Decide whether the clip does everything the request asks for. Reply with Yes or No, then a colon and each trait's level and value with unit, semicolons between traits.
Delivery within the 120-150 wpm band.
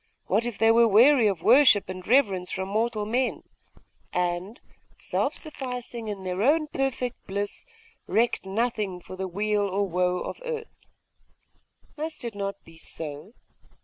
Yes: average, 145 wpm